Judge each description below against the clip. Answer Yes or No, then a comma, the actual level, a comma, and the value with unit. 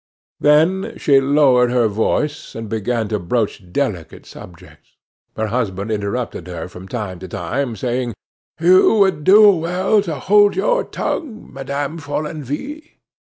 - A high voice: No, low, 135 Hz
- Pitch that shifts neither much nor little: No, wide, 7.6 semitones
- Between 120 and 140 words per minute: Yes, slow, 135 wpm